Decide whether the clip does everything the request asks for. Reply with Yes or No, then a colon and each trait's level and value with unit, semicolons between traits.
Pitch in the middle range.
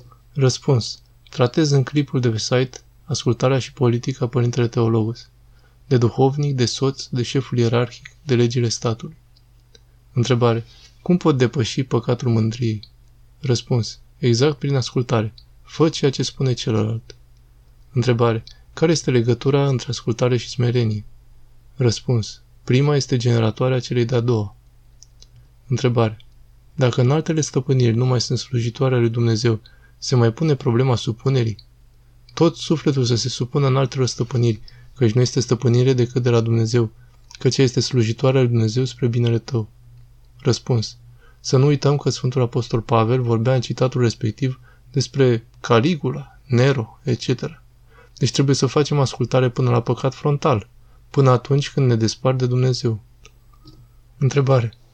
No: low, 120 Hz